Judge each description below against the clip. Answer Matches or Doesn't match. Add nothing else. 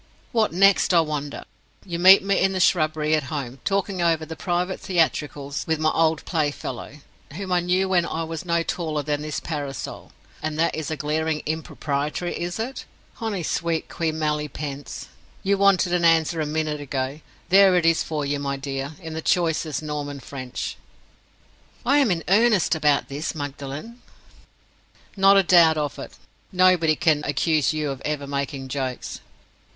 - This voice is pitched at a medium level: Matches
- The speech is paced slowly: Doesn't match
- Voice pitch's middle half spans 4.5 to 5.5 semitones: Doesn't match